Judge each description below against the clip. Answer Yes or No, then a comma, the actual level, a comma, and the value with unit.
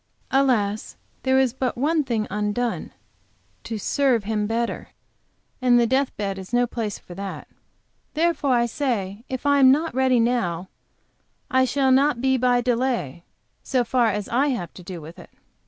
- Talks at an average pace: Yes, average, 170 wpm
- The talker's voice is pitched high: Yes, high, 245 Hz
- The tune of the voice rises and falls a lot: No, average, 4.0 semitones